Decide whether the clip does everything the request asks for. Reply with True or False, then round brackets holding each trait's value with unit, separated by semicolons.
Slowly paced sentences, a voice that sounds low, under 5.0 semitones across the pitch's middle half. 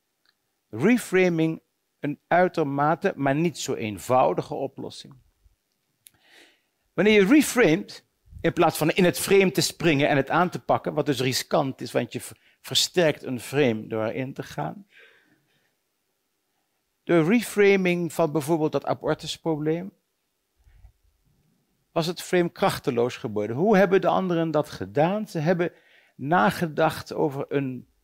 False (125 wpm; 160 Hz; 4.2 semitones)